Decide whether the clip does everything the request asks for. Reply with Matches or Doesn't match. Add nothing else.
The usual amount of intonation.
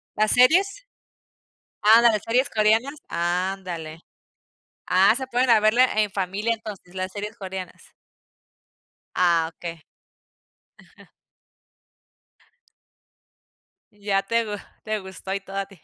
Matches